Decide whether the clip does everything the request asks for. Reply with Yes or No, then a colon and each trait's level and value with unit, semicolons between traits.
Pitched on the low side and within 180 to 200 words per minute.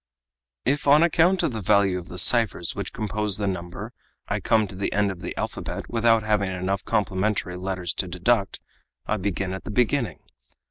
Yes: low, 100 Hz; average, 190 wpm